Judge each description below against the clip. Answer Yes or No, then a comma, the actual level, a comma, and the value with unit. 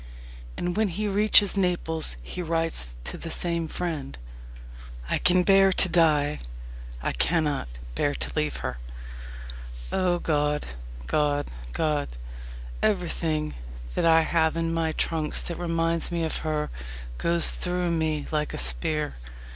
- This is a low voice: No, medium, 165 Hz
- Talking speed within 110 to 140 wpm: Yes, slow, 135 wpm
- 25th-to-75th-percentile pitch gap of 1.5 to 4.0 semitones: Yes, narrow, 2.6 semitones